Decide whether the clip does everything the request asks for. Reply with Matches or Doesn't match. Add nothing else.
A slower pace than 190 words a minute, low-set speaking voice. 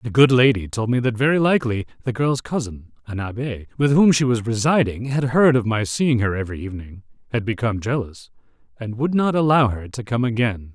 Doesn't match